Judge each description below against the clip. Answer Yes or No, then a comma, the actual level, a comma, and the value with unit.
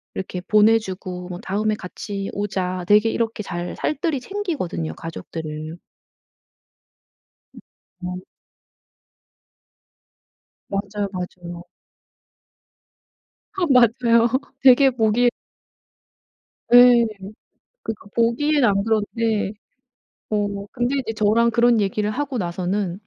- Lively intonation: No, average, 4.3 semitones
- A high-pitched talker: Yes, high, 210 Hz